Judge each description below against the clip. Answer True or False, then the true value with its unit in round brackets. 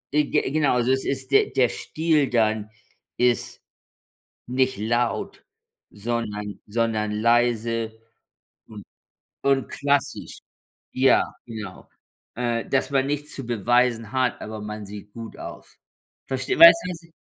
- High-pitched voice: False (120 Hz)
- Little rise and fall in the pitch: False (3.3 semitones)